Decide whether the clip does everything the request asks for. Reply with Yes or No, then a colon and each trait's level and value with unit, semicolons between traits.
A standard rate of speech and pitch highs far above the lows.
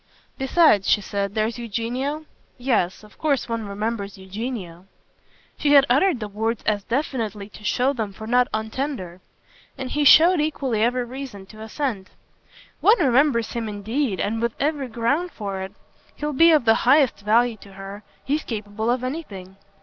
No: average, 165 wpm; average, 4.8 semitones